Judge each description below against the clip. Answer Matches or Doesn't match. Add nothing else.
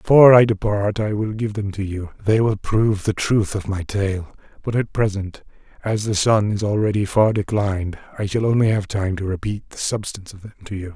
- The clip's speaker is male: Matches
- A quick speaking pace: Matches